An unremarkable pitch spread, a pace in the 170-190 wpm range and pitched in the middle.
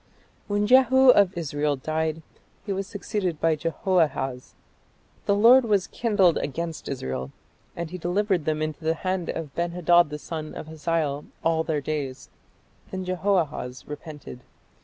No: average, 3.9 semitones; average, 150 wpm; medium, 165 Hz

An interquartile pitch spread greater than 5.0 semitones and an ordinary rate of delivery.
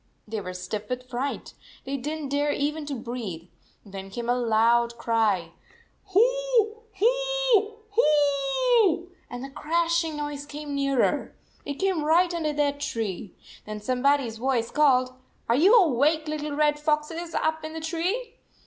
Yes: wide, 5.4 semitones; average, 155 wpm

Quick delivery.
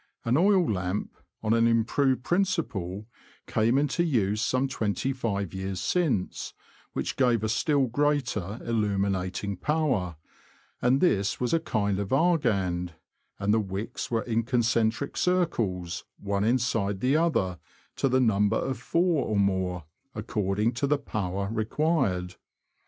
No: average, 140 wpm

